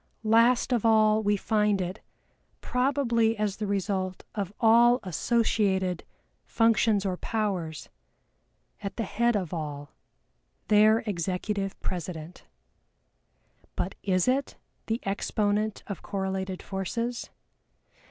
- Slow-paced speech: Yes, slow, 105 wpm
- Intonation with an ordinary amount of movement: Yes, average, 3.1 semitones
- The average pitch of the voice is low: No, high, 205 Hz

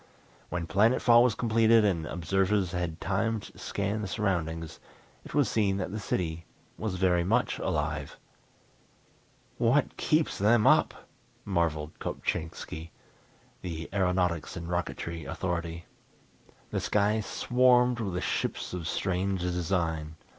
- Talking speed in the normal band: No, slow, 125 wpm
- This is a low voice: Yes, very low, 95 Hz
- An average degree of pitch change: Yes, average, 4.2 semitones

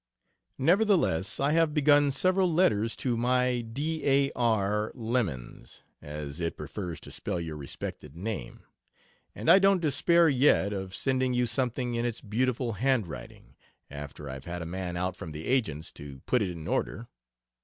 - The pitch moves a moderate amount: No, wide, 7.7 semitones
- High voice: No, low, 115 Hz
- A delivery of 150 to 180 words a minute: Yes, average, 160 wpm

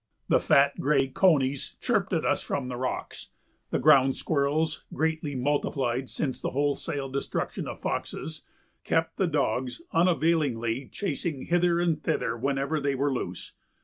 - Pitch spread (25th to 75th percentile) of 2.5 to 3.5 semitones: Yes, average, 3.2 semitones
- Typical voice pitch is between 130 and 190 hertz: Yes, medium, 140 Hz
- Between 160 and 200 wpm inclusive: No, average, 145 wpm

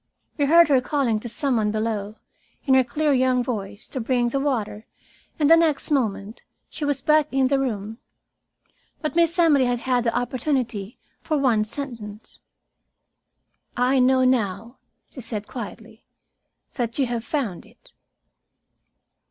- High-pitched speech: Yes, very high, 250 Hz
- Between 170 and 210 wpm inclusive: No, average, 150 wpm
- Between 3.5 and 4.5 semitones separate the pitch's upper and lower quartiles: Yes, average, 3.8 semitones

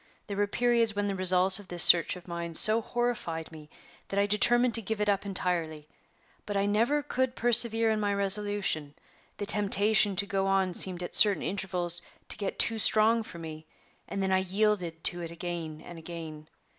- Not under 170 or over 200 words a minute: Yes, average, 195 wpm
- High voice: Yes, high, 195 Hz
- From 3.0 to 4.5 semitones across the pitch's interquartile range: Yes, average, 3.7 semitones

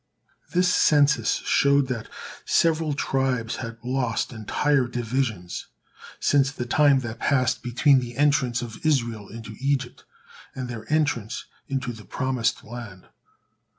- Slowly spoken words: Yes, slow, 125 wpm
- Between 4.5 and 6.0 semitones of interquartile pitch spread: No, average, 3.3 semitones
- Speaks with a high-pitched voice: No, low, 125 Hz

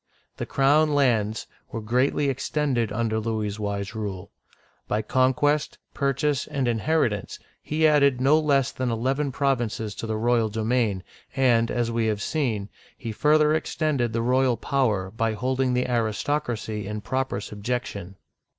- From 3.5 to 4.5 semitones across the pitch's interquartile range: Yes, average, 4.1 semitones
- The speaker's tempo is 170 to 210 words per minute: No, average, 140 wpm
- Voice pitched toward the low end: Yes, low, 120 Hz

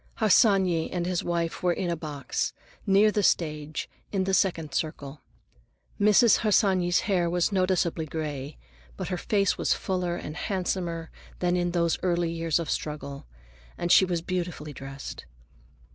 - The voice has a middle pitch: Yes, medium, 175 Hz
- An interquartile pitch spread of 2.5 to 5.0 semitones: Yes, average, 2.8 semitones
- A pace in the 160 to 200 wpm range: No, average, 150 wpm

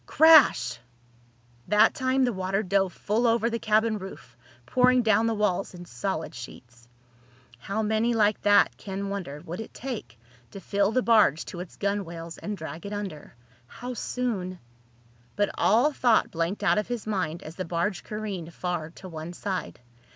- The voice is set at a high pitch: Yes, high, 200 Hz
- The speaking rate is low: No, average, 165 wpm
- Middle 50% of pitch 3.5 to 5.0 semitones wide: Yes, average, 4.3 semitones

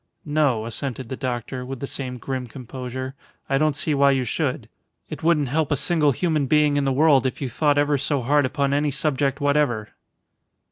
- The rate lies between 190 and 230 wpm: Yes, average, 195 wpm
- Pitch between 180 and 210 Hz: No, medium, 140 Hz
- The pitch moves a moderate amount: No, narrow, 2.3 semitones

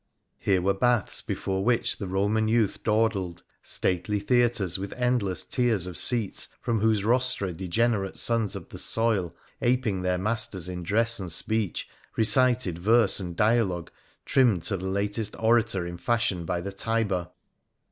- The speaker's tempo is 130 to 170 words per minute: Yes, average, 150 wpm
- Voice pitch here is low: Yes, low, 105 Hz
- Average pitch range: Yes, average, 3.8 semitones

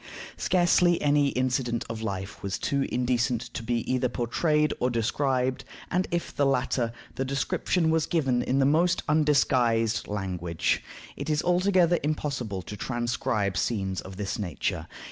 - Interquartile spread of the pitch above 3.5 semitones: Yes, average, 4.8 semitones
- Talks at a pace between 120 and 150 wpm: Yes, average, 145 wpm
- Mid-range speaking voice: No, low, 130 Hz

